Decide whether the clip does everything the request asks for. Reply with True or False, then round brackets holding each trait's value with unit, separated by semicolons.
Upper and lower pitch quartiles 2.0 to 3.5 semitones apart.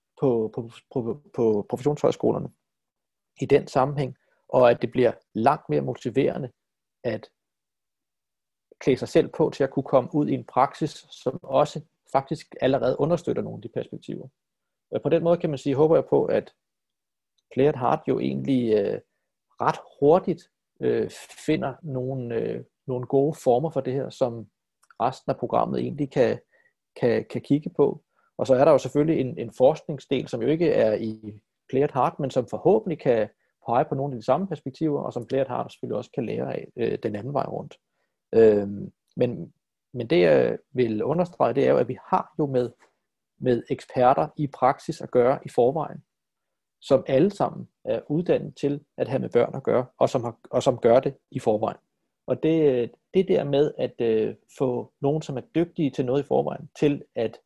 True (3.2 semitones)